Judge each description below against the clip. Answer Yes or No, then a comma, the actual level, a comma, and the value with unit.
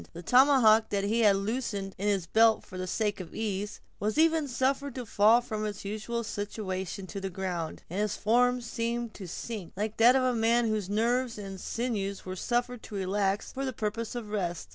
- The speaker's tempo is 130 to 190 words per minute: No, fast, 205 wpm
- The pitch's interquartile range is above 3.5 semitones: No, average, 3.2 semitones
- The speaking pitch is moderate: No, high, 215 Hz